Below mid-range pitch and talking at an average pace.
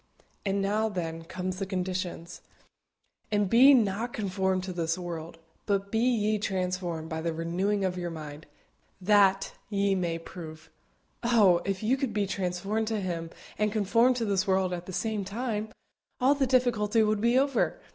No: high, 195 Hz; average, 165 wpm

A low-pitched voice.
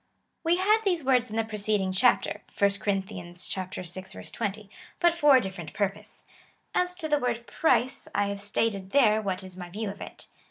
No: high, 210 Hz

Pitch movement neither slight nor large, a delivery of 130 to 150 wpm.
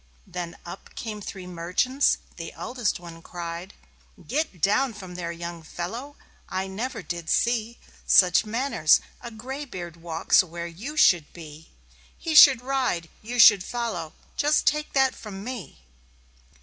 No: wide, 6.4 semitones; average, 140 wpm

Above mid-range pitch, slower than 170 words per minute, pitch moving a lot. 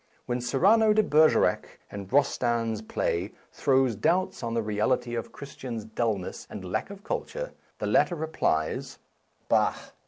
No: low, 120 Hz; average, 155 wpm; wide, 6.3 semitones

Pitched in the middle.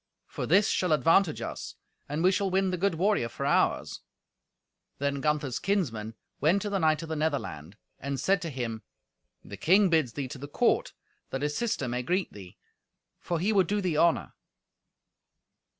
Yes: medium, 160 Hz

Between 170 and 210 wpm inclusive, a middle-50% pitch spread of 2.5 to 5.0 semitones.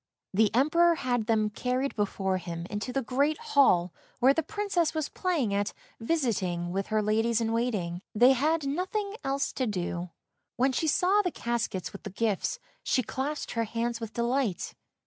No: average, 180 wpm; wide, 5.6 semitones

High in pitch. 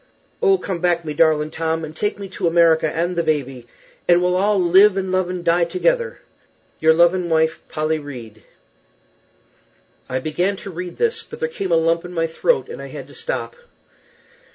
No: medium, 170 Hz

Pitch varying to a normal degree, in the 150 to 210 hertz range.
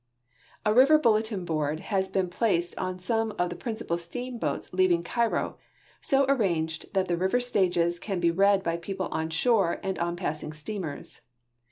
Yes: average, 4.3 semitones; medium, 185 Hz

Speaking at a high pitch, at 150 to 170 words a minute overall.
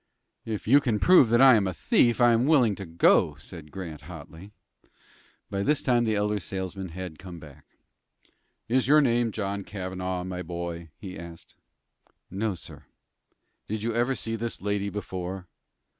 No: low, 100 Hz; average, 165 wpm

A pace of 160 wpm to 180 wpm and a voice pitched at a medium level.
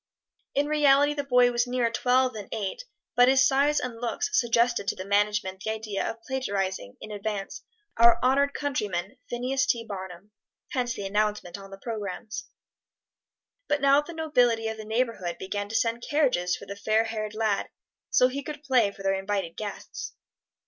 No: average, 175 wpm; high, 230 Hz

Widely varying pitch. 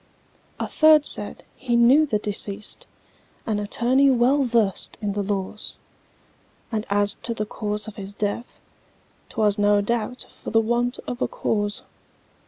No: average, 2.8 semitones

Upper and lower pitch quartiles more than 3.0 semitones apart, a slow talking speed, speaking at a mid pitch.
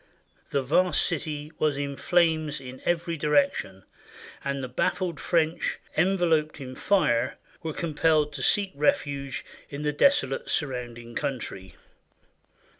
Yes: average, 3.5 semitones; slow, 120 wpm; medium, 150 Hz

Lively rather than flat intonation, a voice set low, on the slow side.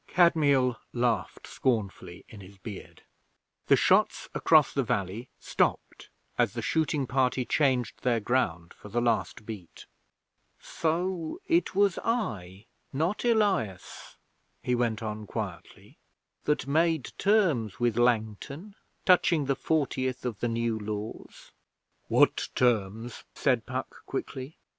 Yes: wide, 6.0 semitones; low, 125 Hz; slow, 120 wpm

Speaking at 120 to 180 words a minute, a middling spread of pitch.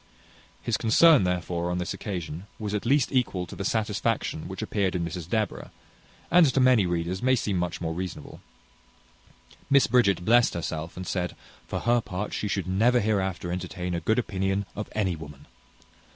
Yes: average, 175 wpm; average, 3.9 semitones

